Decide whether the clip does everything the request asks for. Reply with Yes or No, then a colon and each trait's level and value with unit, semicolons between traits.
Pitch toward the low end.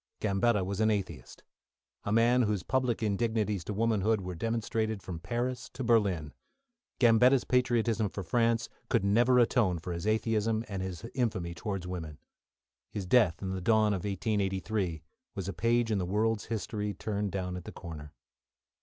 Yes: low, 105 Hz